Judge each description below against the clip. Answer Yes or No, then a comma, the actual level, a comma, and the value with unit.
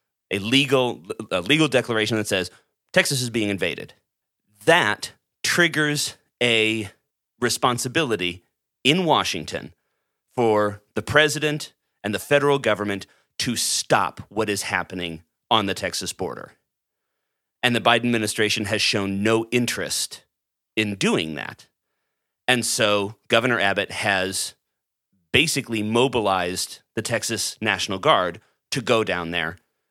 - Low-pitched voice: Yes, low, 110 Hz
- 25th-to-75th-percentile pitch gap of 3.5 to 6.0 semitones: Yes, average, 4.0 semitones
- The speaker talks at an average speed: No, slow, 120 wpm